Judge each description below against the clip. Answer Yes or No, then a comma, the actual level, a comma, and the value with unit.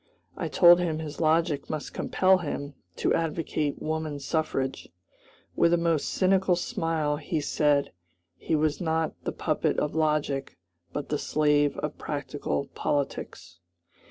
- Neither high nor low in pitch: Yes, medium, 155 Hz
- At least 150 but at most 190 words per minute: No, slow, 135 wpm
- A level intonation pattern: Yes, narrow, 2.1 semitones